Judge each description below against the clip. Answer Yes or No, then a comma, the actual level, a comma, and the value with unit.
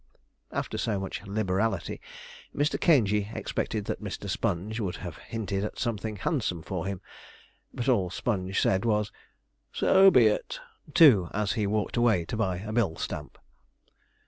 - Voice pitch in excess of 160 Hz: No, low, 105 Hz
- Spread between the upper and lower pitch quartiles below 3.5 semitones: Yes, average, 3.1 semitones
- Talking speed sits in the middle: Yes, average, 150 wpm